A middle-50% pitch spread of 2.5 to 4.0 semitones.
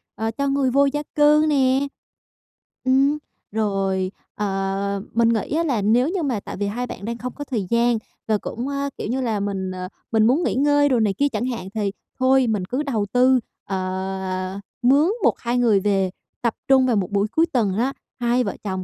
No: average, 5.0 semitones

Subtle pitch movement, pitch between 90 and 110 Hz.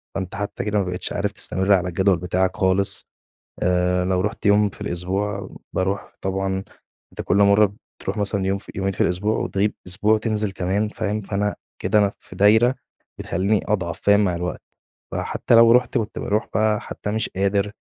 Yes: narrow, 2.0 semitones; low, 100 Hz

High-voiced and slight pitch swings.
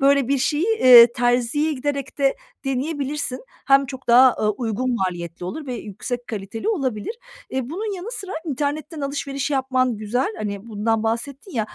No: very high, 260 Hz; average, 3.6 semitones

